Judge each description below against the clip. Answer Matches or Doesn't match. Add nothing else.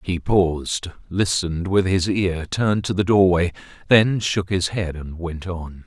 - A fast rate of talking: Doesn't match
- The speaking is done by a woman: Doesn't match